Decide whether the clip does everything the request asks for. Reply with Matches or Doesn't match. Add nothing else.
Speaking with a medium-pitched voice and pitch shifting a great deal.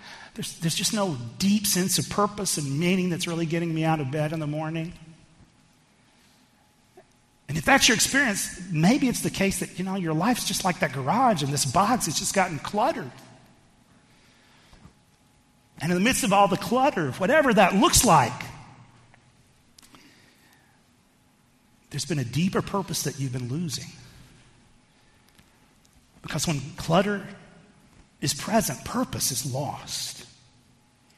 Matches